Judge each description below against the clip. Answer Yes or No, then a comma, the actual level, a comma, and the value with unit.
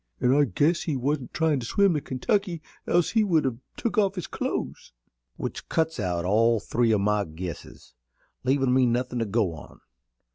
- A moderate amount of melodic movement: No, wide, 6.7 semitones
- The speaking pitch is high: No, low, 130 Hz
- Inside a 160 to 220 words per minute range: Yes, average, 185 wpm